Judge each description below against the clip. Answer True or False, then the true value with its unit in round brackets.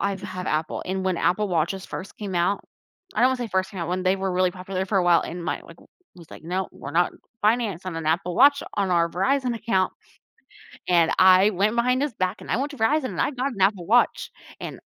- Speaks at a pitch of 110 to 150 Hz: False (190 Hz)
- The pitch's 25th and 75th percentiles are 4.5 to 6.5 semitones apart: False (3.8 semitones)